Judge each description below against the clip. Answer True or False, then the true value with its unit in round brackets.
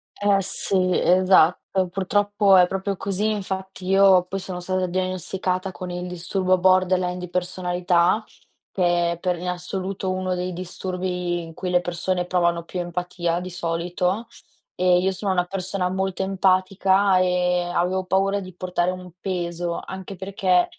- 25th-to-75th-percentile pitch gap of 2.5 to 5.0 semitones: False (1.2 semitones)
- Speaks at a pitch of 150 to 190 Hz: True (185 Hz)